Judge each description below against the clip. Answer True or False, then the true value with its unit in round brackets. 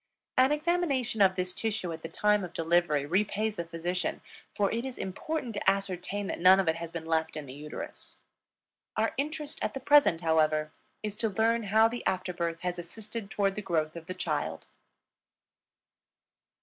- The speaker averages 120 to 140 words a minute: False (175 wpm)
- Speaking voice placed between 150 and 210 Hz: True (190 Hz)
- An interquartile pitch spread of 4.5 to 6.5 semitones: True (4.9 semitones)